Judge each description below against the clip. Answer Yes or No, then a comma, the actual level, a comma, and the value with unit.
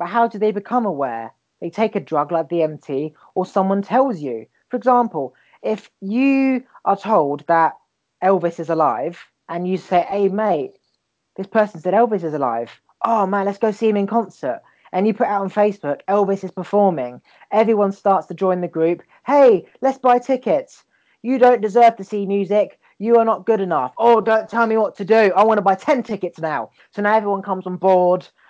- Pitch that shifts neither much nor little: Yes, average, 3.8 semitones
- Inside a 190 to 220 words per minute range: Yes, average, 200 wpm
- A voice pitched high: Yes, high, 200 Hz